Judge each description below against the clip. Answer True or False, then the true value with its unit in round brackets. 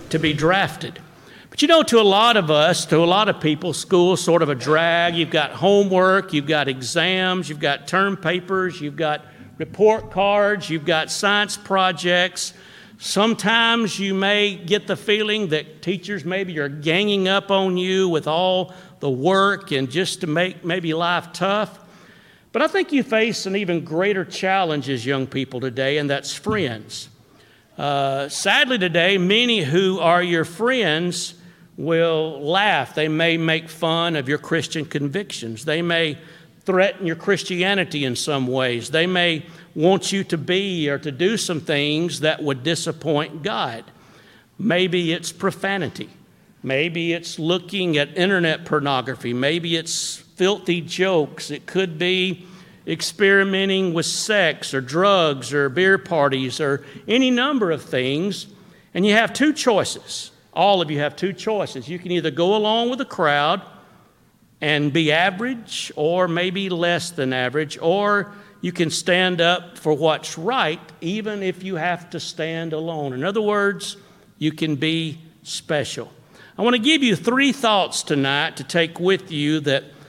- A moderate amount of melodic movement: True (3.9 semitones)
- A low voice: False (175 Hz)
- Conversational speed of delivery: True (160 wpm)